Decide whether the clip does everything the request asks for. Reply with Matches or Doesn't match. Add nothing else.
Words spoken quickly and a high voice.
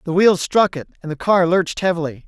Doesn't match